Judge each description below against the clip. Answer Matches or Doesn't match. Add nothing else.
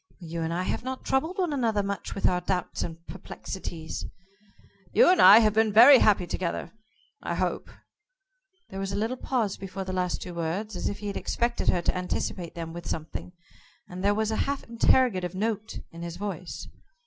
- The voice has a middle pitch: Doesn't match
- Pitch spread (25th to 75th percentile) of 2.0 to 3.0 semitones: Doesn't match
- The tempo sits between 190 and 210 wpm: Matches